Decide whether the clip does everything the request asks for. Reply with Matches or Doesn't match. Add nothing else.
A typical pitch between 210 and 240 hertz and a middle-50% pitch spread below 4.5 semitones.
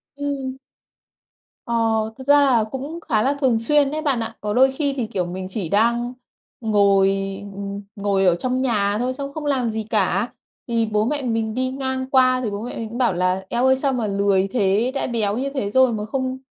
Matches